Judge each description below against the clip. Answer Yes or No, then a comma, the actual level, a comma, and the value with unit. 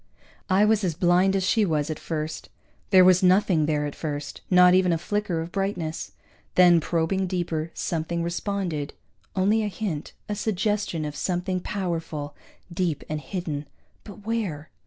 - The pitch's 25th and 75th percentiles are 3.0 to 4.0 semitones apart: Yes, average, 3.5 semitones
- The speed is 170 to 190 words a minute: No, average, 155 wpm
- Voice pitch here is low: No, medium, 180 Hz